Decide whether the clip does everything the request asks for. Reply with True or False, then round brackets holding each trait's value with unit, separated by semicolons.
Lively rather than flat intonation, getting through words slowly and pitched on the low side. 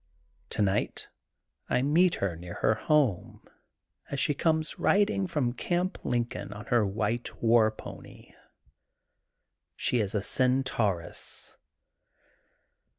True (6.3 semitones; 110 wpm; 120 Hz)